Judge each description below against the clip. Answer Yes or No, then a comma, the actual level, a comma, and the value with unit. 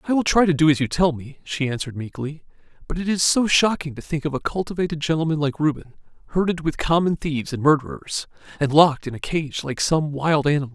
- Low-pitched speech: No, medium, 155 Hz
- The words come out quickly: Yes, fast, 225 wpm